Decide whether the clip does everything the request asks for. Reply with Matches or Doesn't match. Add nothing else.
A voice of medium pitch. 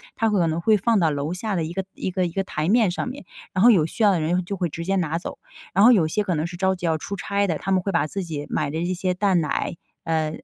Matches